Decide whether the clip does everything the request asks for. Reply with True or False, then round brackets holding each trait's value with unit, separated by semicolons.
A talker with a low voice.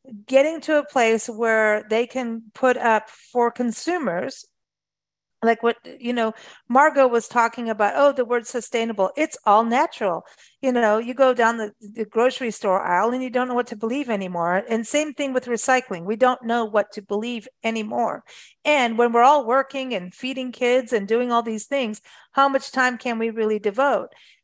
False (235 Hz)